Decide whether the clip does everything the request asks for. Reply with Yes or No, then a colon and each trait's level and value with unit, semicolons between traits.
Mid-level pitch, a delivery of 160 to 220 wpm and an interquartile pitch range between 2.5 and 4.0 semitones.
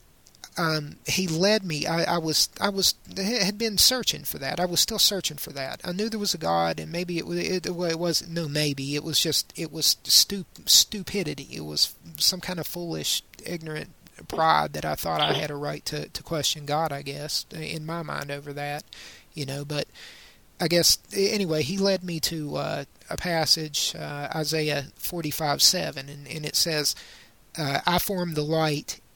Yes: medium, 160 Hz; average, 195 wpm; average, 3.3 semitones